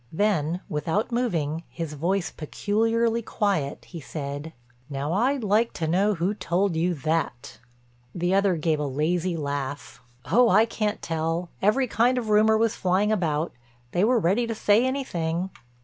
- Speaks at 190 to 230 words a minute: No, average, 150 wpm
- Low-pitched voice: No, medium, 180 Hz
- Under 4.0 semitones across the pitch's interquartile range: No, average, 5.2 semitones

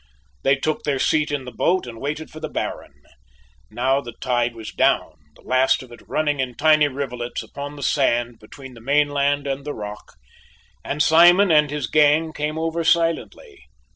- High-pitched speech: No, medium, 140 Hz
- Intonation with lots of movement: No, average, 3.5 semitones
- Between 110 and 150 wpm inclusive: No, average, 180 wpm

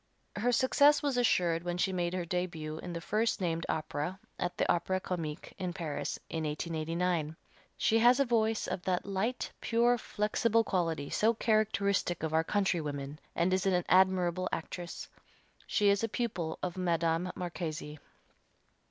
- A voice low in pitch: No, medium, 180 Hz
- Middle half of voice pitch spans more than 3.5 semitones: Yes, average, 4.1 semitones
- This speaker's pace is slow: No, average, 155 wpm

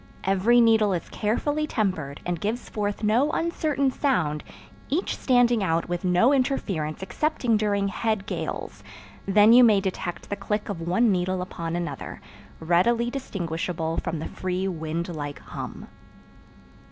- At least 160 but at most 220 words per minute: No, average, 140 wpm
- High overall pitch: Yes, high, 200 Hz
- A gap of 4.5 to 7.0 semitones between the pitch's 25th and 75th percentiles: Yes, wide, 5.4 semitones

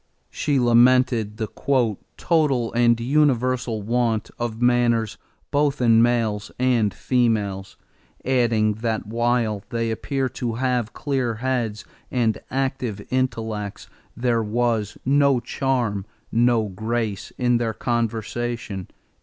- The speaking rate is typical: No, slow, 110 wpm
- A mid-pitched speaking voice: No, low, 120 Hz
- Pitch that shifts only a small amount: Yes, narrow, 2.3 semitones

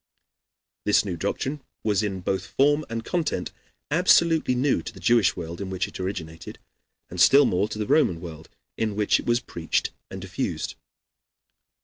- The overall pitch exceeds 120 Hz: No, low, 105 Hz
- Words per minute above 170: No, average, 165 wpm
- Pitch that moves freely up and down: Yes, wide, 6.5 semitones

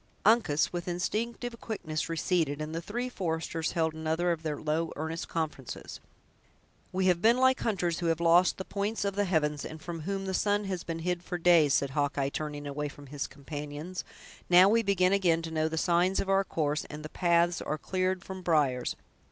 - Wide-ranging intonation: No, average, 3.5 semitones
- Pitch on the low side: No, medium, 170 Hz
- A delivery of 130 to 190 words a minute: No, average, 200 wpm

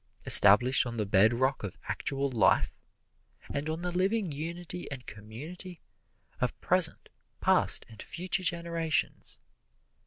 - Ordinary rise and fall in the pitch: No, wide, 6.7 semitones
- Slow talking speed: Yes, slow, 120 wpm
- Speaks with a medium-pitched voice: Yes, medium, 145 Hz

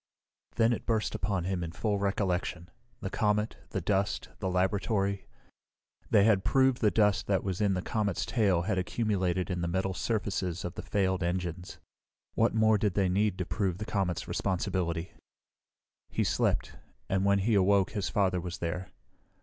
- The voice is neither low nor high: No, very low, 95 Hz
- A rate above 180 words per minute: No, average, 170 wpm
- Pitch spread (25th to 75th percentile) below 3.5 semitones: Yes, narrow, 2.4 semitones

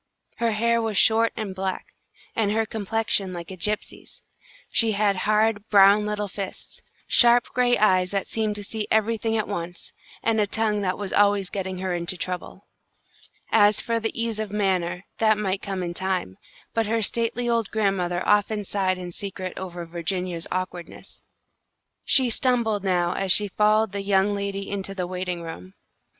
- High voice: Yes, high, 200 Hz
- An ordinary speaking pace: Yes, average, 170 wpm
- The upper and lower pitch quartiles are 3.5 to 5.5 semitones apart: No, average, 2.9 semitones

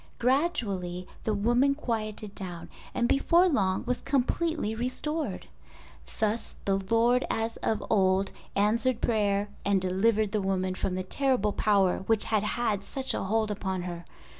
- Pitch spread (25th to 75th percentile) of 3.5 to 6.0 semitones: Yes, average, 3.8 semitones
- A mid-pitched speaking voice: No, high, 215 Hz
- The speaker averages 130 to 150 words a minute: Yes, average, 145 wpm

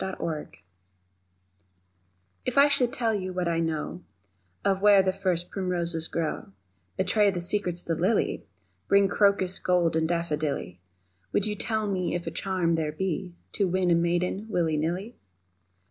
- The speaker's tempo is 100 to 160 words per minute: Yes, average, 155 wpm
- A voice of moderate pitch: Yes, medium, 180 Hz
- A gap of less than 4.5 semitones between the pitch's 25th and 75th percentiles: Yes, average, 2.9 semitones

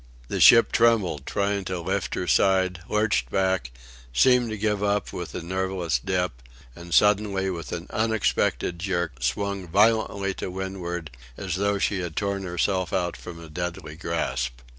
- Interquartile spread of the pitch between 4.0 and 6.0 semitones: No, average, 2.8 semitones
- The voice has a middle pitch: No, very low, 95 Hz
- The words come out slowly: No, average, 160 wpm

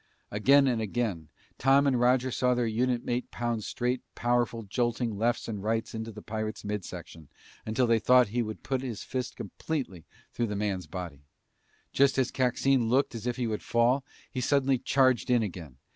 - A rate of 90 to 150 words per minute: No, average, 185 wpm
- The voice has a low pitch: Yes, low, 120 Hz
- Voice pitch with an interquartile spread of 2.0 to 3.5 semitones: Yes, average, 3.0 semitones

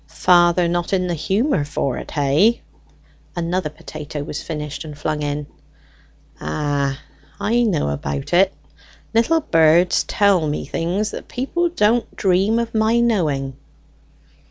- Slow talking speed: Yes, slow, 130 wpm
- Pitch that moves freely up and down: Yes, wide, 6.1 semitones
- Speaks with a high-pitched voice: No, medium, 175 Hz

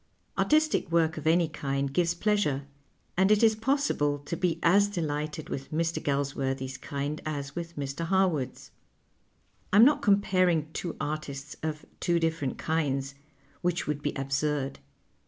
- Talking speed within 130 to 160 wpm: Yes, average, 145 wpm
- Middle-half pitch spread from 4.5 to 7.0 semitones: No, average, 3.8 semitones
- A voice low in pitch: No, medium, 155 Hz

